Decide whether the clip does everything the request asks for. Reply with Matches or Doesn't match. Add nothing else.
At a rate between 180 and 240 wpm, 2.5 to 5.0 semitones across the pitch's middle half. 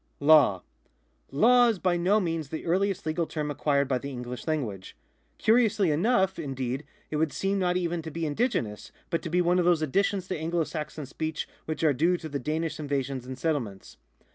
Matches